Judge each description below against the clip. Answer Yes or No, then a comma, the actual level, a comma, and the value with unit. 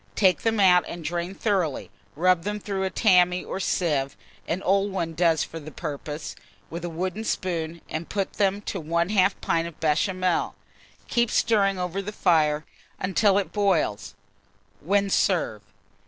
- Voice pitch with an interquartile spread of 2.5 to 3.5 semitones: Yes, average, 3.1 semitones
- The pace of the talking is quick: No, average, 155 wpm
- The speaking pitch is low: No, medium, 180 Hz